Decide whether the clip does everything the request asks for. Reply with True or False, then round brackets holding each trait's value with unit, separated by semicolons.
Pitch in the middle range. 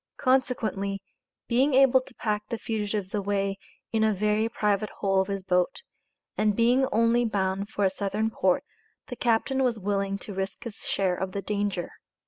False (210 Hz)